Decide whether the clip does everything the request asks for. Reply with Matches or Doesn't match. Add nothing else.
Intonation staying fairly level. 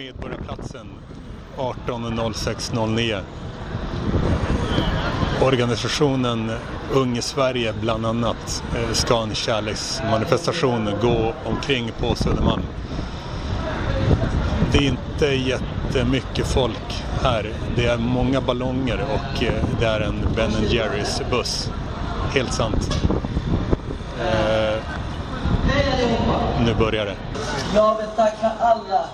Doesn't match